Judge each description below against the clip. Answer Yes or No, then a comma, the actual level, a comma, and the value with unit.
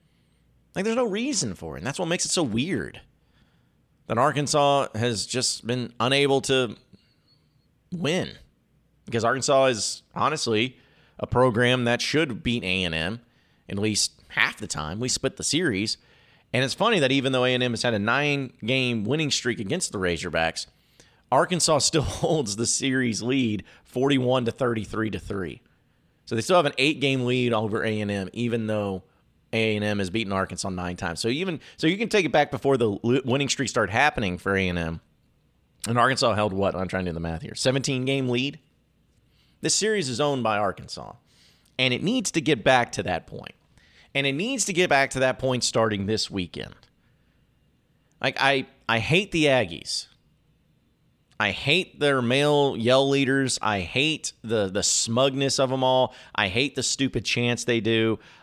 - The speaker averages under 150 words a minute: No, average, 175 wpm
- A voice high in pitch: No, low, 125 Hz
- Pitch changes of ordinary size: Yes, average, 4.1 semitones